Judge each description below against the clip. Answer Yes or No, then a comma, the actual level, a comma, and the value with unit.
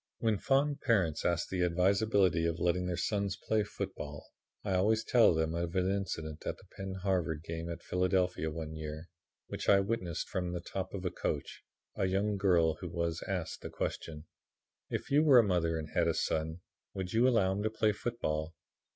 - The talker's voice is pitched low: Yes, very low, 90 Hz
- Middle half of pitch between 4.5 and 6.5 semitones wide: No, average, 3.3 semitones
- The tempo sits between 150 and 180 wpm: No, average, 190 wpm